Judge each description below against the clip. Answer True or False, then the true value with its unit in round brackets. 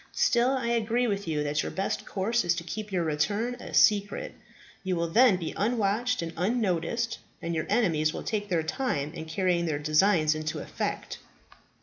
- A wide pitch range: True (5.8 semitones)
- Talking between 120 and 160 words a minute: False (185 wpm)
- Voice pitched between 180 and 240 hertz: True (190 Hz)